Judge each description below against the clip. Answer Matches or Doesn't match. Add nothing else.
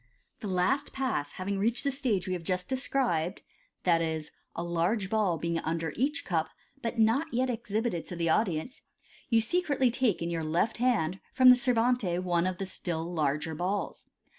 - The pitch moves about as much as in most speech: Doesn't match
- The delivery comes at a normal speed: Matches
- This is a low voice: Doesn't match